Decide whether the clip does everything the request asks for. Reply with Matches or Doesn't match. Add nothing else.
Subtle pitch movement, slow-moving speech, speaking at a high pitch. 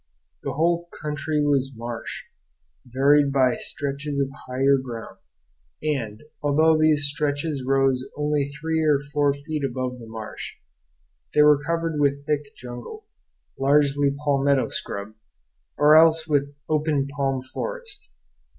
Doesn't match